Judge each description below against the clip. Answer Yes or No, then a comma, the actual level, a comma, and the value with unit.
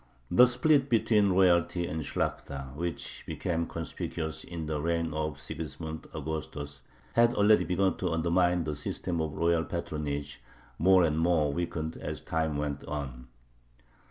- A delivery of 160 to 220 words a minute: No, average, 140 wpm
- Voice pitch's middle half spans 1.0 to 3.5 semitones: Yes, average, 2.8 semitones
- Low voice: Yes, very low, 80 Hz